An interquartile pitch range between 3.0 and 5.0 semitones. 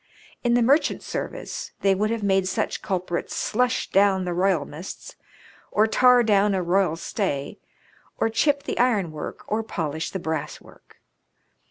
Yes: average, 4.4 semitones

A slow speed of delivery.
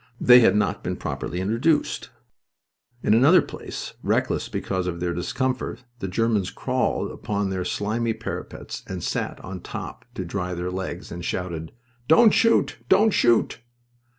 No: average, 150 wpm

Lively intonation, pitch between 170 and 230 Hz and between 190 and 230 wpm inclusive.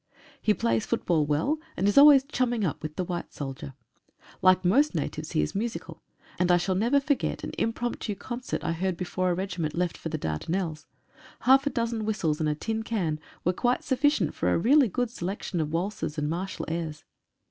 Yes: wide, 6.6 semitones; medium, 185 Hz; average, 195 wpm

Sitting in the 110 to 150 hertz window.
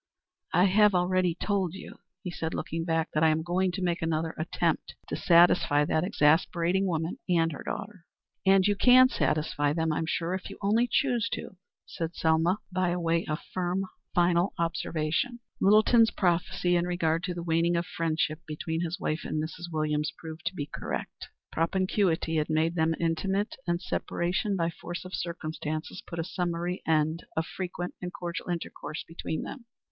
No: medium, 170 Hz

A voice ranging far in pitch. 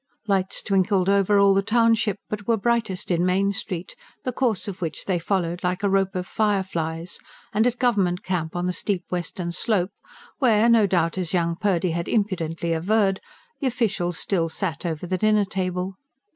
No: average, 3.0 semitones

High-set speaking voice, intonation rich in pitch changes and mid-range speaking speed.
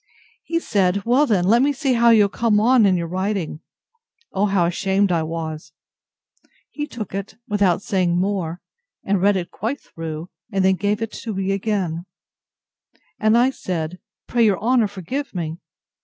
No: high, 195 Hz; average, 3.9 semitones; average, 160 wpm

